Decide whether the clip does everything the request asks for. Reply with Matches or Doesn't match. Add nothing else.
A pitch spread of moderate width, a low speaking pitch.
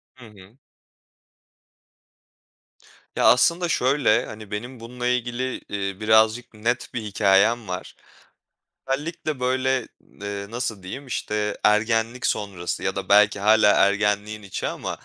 Matches